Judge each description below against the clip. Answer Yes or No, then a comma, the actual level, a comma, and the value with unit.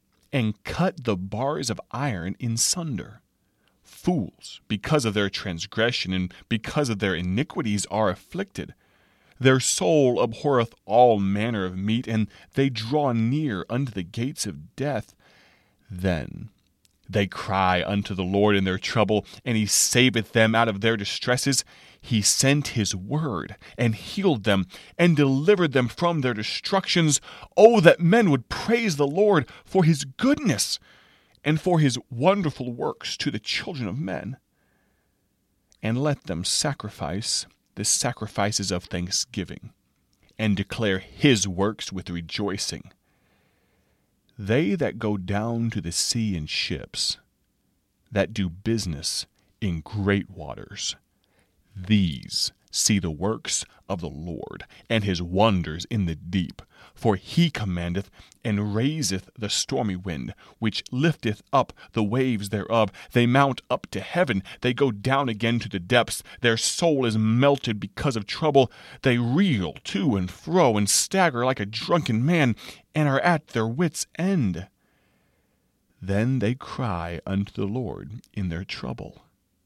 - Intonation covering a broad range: Yes, wide, 5.7 semitones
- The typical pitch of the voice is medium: No, low, 110 Hz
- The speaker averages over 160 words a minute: No, average, 140 wpm